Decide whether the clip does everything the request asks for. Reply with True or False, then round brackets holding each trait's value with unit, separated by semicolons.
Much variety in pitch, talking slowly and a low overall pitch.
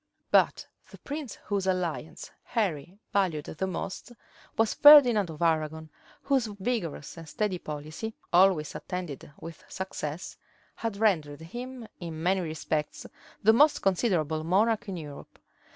False (5.7 semitones; 130 wpm; 185 Hz)